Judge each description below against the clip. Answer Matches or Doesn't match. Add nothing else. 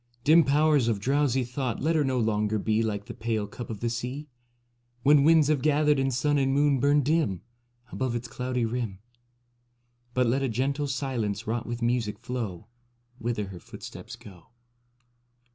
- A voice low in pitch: Matches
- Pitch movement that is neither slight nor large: Matches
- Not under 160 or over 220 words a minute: Matches